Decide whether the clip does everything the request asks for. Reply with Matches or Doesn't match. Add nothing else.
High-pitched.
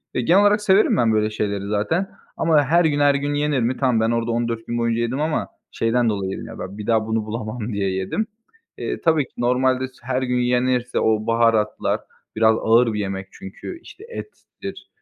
Doesn't match